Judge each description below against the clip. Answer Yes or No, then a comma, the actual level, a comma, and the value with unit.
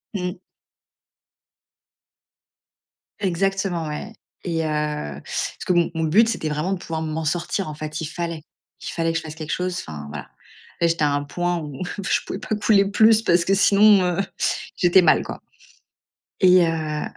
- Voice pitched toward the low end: No, medium, 170 Hz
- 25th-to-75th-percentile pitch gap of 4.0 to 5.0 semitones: No, average, 3.5 semitones